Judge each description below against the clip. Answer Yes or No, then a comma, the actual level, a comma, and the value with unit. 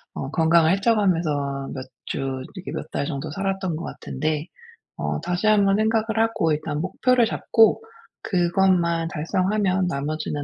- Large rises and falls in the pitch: No, average, 4.4 semitones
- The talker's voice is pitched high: No, medium, 175 Hz